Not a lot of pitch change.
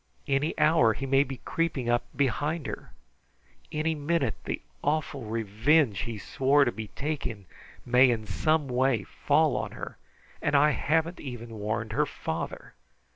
No: average, 4.6 semitones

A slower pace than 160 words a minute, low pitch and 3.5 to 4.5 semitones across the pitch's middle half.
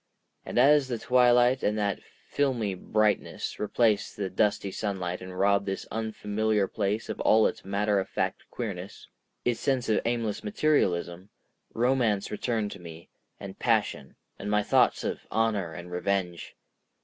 No: average, 150 wpm; low, 105 Hz; average, 3.0 semitones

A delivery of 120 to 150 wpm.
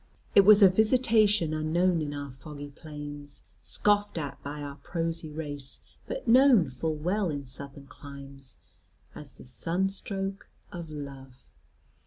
Yes: slow, 135 wpm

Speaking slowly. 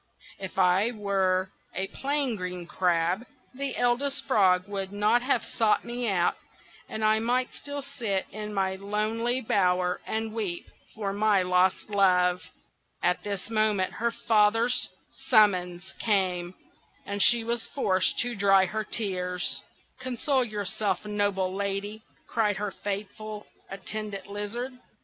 Yes: slow, 130 wpm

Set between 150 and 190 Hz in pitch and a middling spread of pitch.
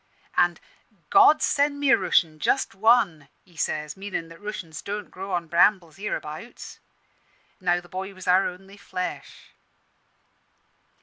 Yes: medium, 185 Hz; average, 3.6 semitones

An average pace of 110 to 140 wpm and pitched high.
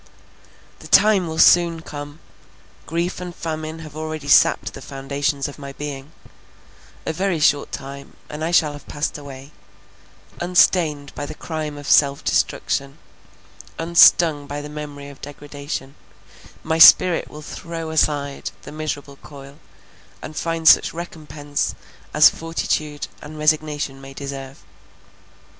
No: slow, 135 wpm; medium, 150 Hz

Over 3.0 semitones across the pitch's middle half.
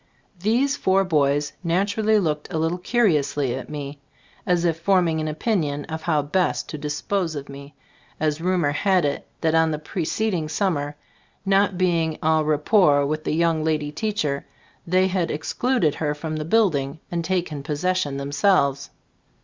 Yes: average, 3.9 semitones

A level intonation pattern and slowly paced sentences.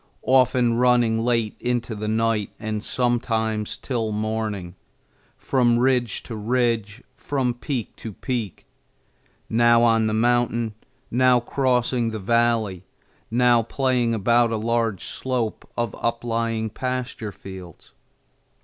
Yes: narrow, 1.8 semitones; slow, 115 wpm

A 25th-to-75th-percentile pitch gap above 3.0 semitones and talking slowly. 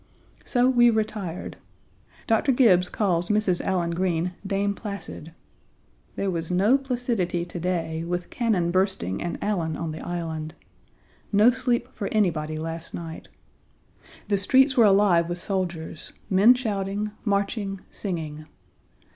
Yes: average, 3.9 semitones; slow, 130 wpm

